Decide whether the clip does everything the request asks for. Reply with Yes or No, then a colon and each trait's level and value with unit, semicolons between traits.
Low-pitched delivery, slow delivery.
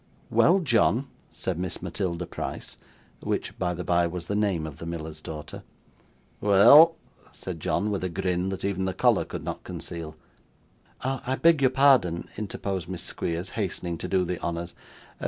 No: very low, 90 Hz; average, 165 wpm